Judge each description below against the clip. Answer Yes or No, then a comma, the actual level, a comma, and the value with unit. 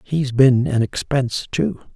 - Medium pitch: No, low, 130 Hz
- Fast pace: No, average, 155 wpm